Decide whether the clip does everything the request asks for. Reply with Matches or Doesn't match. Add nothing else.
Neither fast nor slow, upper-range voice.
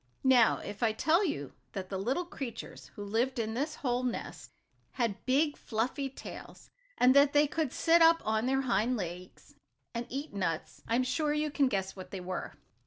Matches